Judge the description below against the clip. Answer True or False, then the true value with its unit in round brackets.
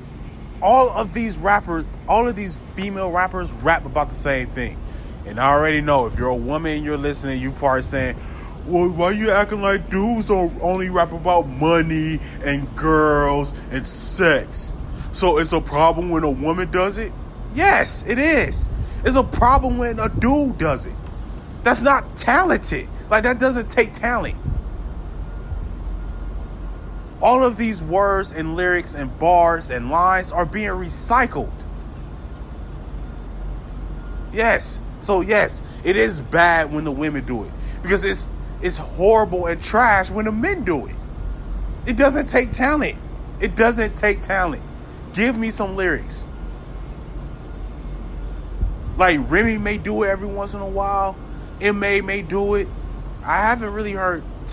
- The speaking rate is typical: True (150 wpm)